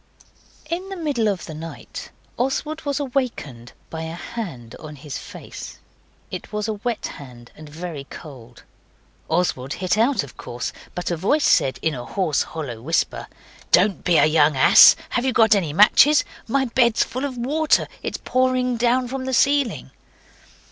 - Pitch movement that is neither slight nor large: No, wide, 9.0 semitones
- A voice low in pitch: No, high, 200 Hz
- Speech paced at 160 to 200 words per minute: Yes, average, 170 wpm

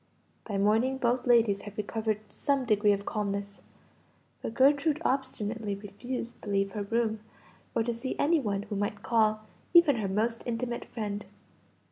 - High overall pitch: Yes, high, 220 Hz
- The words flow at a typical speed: Yes, average, 155 wpm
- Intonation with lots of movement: No, average, 3.1 semitones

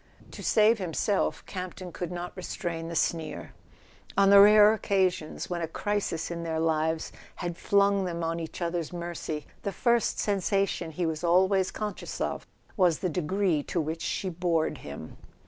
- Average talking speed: Yes, average, 165 wpm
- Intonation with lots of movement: No, average, 3.2 semitones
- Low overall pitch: No, medium, 175 Hz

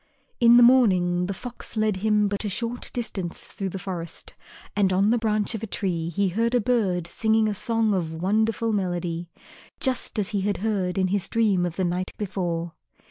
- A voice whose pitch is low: No, high, 200 Hz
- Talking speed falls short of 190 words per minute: No, average, 195 wpm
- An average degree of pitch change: Yes, average, 3.6 semitones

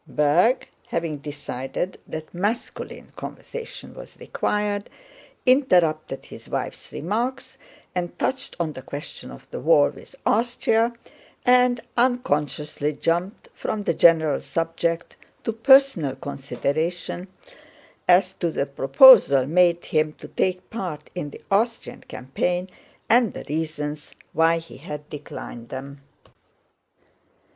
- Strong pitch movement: Yes, wide, 6.6 semitones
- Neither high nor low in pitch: Yes, medium, 170 Hz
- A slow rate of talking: Yes, slow, 115 wpm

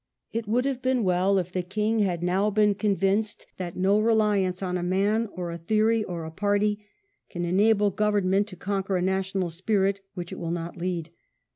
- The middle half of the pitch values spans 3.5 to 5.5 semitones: No, average, 2.8 semitones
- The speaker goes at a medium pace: Yes, average, 190 wpm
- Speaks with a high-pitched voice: Yes, high, 195 Hz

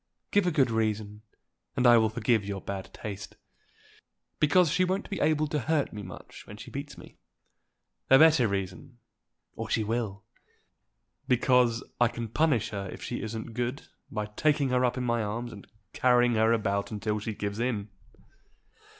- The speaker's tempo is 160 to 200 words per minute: Yes, average, 170 wpm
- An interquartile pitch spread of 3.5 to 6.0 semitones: Yes, average, 4.0 semitones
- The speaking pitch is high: No, low, 115 Hz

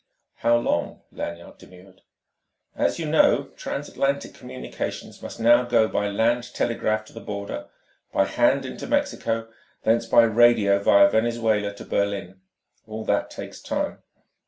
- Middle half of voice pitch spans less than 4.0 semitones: Yes, average, 2.9 semitones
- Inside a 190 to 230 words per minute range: No, slow, 135 wpm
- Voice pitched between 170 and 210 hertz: No, low, 110 Hz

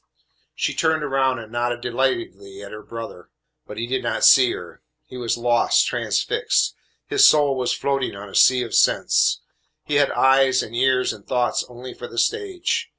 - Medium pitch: No, low, 125 Hz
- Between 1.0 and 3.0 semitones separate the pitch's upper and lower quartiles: Yes, narrow, 2.4 semitones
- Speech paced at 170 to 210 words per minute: Yes, average, 180 wpm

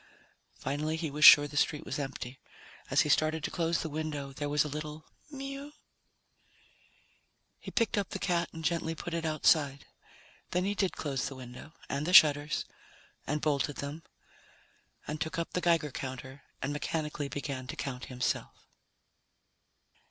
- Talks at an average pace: Yes, average, 160 wpm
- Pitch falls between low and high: Yes, medium, 150 Hz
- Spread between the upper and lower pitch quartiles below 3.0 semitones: Yes, narrow, 2.5 semitones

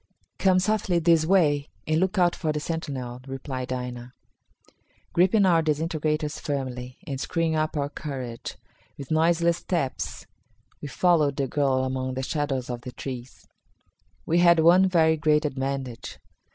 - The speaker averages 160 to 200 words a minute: No, average, 145 wpm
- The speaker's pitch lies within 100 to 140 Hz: No, medium, 150 Hz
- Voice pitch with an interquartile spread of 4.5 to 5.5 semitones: No, average, 4.1 semitones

